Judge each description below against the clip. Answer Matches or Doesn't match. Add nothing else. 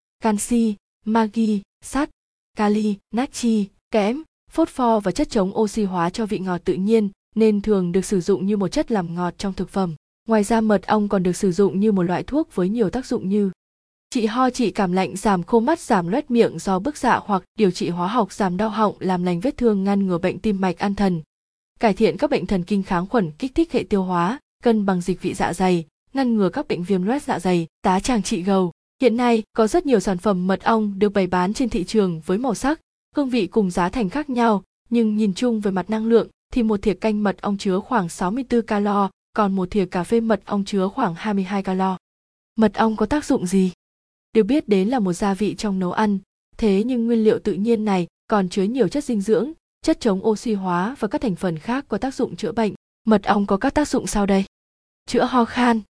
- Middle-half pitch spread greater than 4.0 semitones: Doesn't match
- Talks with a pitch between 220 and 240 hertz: Doesn't match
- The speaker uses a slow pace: Doesn't match